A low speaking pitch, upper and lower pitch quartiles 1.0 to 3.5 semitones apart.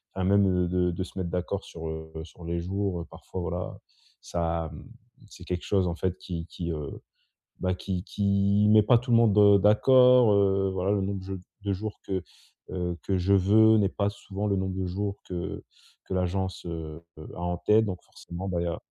Yes: very low, 95 Hz; narrow, 2.4 semitones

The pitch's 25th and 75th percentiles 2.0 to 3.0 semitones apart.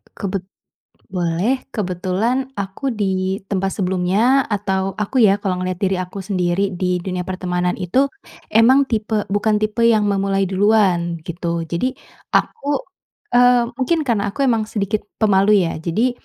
No: average, 3.4 semitones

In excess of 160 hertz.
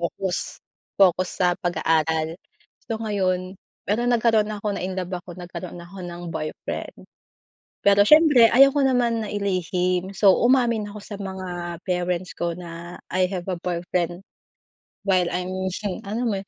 Yes: medium, 185 Hz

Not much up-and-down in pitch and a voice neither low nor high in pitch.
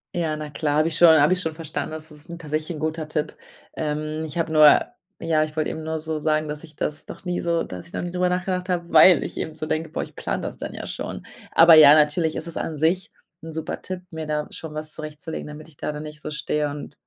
Yes: narrow, 1.4 semitones; medium, 155 Hz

